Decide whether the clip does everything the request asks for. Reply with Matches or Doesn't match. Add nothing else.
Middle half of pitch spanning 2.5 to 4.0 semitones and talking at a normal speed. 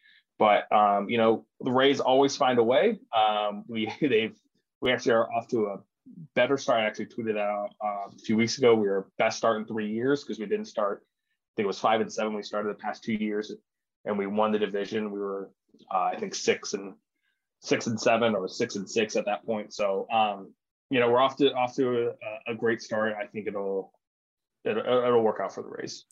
Doesn't match